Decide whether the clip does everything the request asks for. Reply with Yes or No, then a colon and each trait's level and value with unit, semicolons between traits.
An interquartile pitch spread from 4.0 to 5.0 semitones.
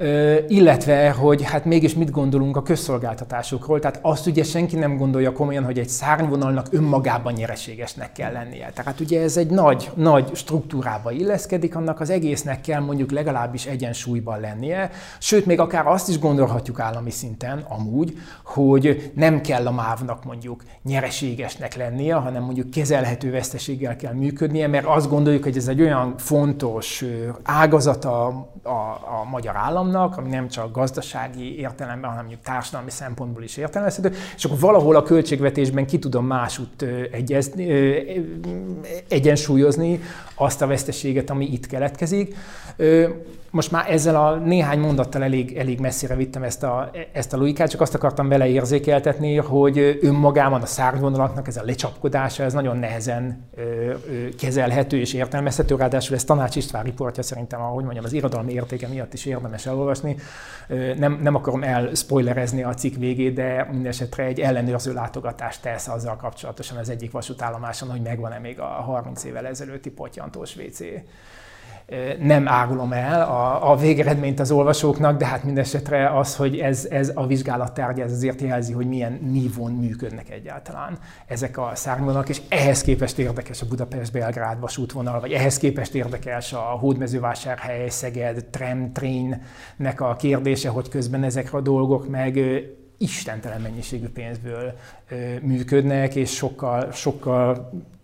No: average, 2.8 semitones